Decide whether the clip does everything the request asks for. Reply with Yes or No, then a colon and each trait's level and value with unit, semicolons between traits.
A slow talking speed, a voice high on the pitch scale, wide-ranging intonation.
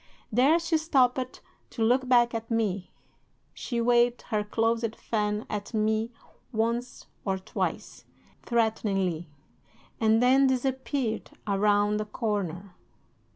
No: slow, 110 wpm; high, 225 Hz; average, 2.9 semitones